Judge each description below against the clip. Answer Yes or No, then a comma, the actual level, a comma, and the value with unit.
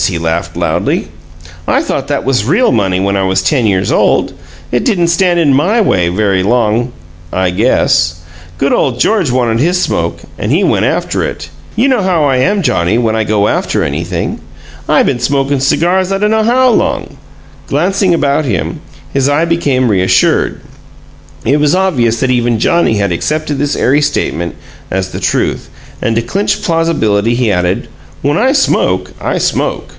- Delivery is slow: No, average, 175 wpm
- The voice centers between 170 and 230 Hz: No, low, 130 Hz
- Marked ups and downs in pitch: Yes, wide, 8.4 semitones